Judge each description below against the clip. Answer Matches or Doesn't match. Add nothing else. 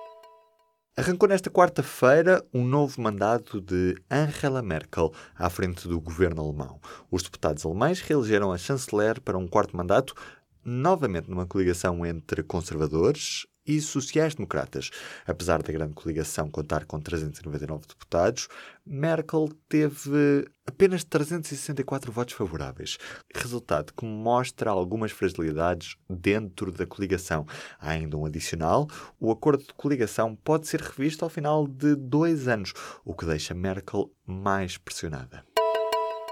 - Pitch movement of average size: Doesn't match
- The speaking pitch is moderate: Doesn't match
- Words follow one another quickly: Doesn't match